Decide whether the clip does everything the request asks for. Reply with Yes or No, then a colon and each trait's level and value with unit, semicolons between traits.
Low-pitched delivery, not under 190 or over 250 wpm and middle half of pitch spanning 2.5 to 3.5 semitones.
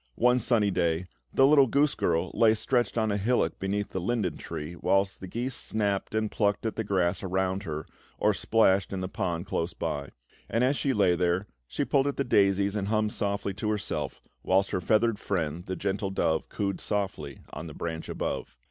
Yes: low, 100 Hz; average, 200 wpm; average, 3.2 semitones